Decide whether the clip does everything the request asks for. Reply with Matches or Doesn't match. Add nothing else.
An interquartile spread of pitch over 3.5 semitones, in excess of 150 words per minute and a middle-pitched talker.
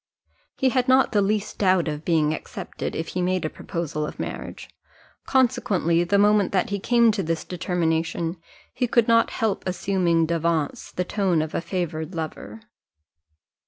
Matches